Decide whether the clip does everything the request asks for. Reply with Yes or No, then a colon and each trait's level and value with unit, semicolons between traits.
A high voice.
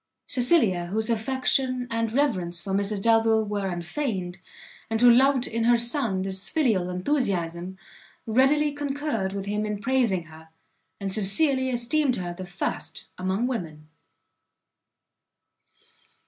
Yes: high, 220 Hz